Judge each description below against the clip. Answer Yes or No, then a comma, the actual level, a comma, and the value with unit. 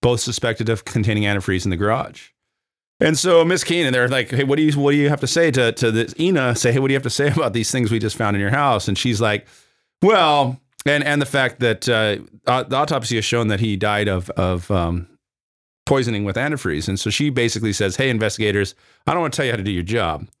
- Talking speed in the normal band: No, fast, 255 wpm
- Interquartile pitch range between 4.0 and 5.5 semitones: Yes, average, 4.9 semitones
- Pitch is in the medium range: No, low, 120 Hz